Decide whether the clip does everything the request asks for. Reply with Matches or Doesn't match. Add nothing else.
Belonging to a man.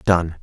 Matches